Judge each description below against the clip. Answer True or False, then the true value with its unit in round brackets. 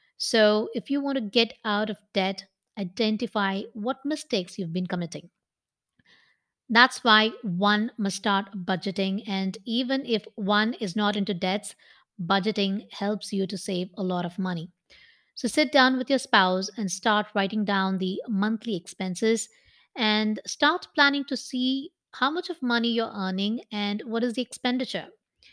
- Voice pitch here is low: False (210 Hz)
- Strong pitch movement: False (3.5 semitones)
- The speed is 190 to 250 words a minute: False (155 wpm)